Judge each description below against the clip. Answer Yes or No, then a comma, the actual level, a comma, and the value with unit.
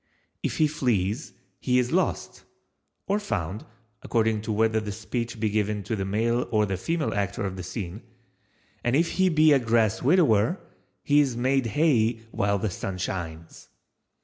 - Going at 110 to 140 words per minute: No, average, 160 wpm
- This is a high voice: No, low, 115 Hz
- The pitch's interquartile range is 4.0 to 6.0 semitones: Yes, average, 4.5 semitones